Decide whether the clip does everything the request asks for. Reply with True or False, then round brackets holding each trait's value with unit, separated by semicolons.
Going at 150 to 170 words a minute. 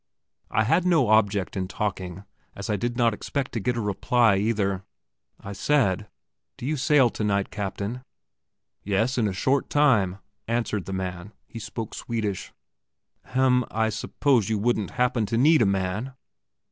True (160 wpm)